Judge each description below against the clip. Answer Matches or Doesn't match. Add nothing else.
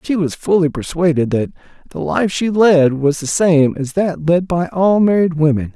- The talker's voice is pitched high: Doesn't match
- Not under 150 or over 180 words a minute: Doesn't match